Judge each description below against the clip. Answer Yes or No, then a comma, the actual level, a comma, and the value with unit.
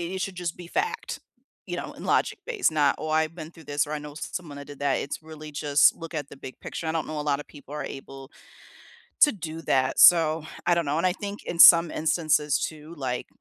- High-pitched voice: No, medium, 155 Hz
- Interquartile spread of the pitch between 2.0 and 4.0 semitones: Yes, narrow, 2.6 semitones